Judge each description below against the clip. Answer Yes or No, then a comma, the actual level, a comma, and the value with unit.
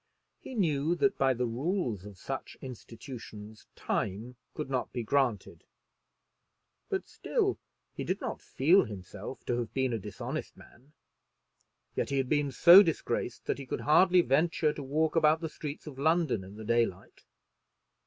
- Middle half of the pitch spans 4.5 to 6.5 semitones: Yes, wide, 5.4 semitones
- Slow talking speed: No, average, 160 wpm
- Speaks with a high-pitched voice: No, low, 135 Hz